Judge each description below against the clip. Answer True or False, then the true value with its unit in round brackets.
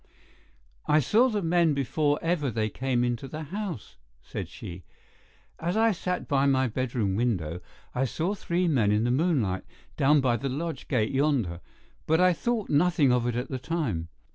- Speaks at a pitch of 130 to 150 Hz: True (140 Hz)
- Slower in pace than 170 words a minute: False (175 wpm)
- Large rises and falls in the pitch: True (5.8 semitones)